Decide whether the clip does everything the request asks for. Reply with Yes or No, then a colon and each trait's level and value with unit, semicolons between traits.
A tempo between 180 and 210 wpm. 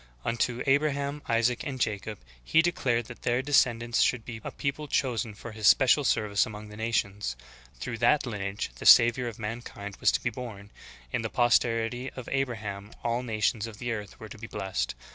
Yes: average, 190 wpm